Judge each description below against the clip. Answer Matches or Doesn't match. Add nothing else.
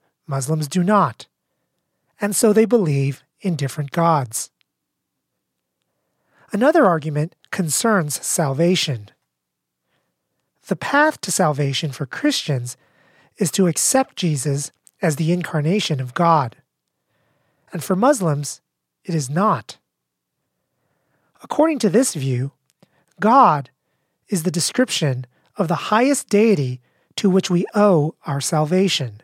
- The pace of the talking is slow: Matches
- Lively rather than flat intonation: Matches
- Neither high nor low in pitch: Matches